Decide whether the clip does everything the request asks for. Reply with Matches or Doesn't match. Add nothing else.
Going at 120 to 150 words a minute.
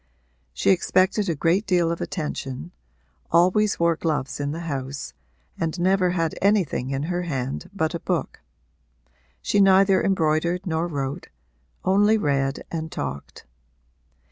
Matches